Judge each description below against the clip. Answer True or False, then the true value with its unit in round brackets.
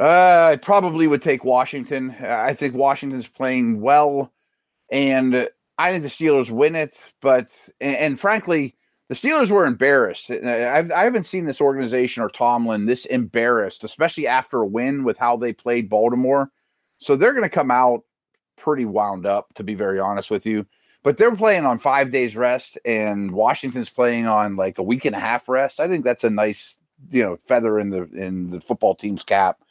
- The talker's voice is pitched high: False (125 Hz)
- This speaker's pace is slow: False (185 wpm)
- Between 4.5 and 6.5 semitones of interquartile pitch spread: False (3.5 semitones)